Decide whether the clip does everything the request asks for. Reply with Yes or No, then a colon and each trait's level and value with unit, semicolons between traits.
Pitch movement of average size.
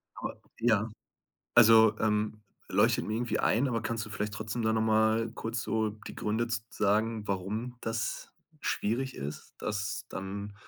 No: narrow, 1.4 semitones